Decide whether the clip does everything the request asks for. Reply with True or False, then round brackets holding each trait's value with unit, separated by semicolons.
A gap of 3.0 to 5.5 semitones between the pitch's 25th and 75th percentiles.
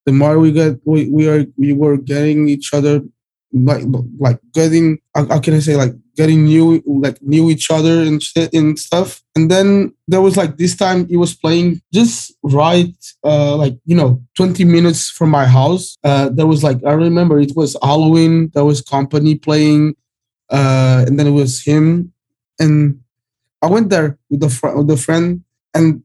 False (2.5 semitones)